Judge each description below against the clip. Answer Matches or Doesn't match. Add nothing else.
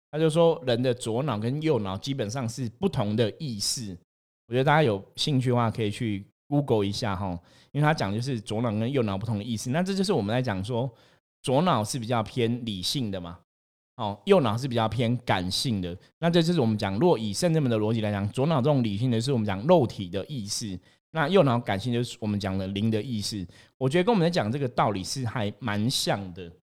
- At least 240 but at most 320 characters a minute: Doesn't match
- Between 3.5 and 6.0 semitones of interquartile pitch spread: Matches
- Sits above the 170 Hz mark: Doesn't match